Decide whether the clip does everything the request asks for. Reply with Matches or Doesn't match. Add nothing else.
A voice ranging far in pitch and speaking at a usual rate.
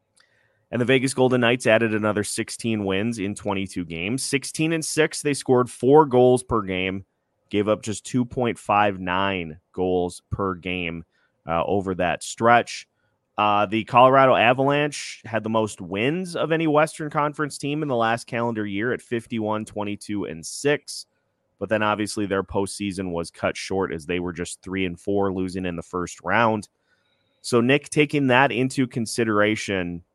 Doesn't match